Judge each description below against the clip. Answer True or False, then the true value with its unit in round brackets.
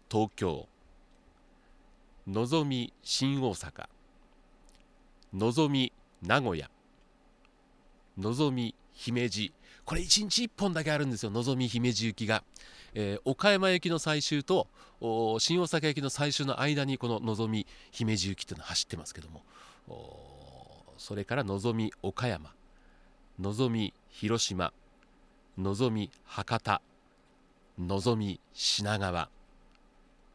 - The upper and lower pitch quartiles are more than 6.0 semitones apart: False (5.6 semitones)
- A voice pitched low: True (115 Hz)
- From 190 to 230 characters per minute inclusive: True (210 characters per minute)